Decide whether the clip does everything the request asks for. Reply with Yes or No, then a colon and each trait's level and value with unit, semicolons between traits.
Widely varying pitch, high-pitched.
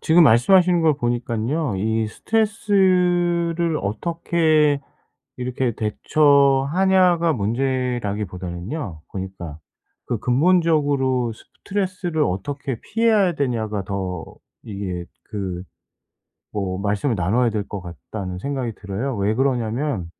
No: wide, 8.1 semitones; low, 125 Hz